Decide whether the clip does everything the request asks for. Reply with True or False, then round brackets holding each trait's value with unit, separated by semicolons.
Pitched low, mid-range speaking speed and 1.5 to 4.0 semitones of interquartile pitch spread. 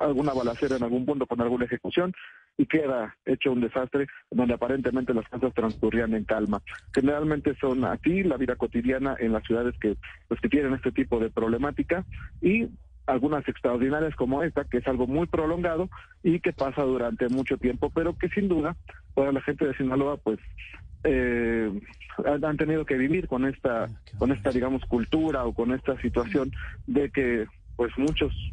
True (130 Hz; 170 wpm; 3.5 semitones)